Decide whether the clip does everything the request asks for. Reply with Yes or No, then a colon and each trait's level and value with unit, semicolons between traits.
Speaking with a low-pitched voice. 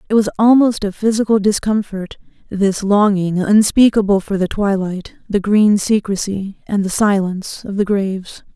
No: high, 205 Hz